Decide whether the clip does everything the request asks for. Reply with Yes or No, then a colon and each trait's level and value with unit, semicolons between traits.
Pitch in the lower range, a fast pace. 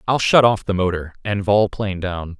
Yes: low, 100 Hz; fast, 225 wpm